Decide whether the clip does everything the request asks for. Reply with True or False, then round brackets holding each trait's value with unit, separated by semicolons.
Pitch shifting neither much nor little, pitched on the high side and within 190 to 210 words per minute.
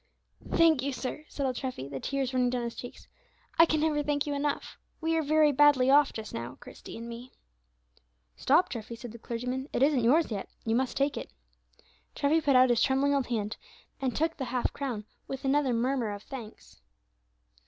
True (3.4 semitones; 265 Hz; 195 wpm)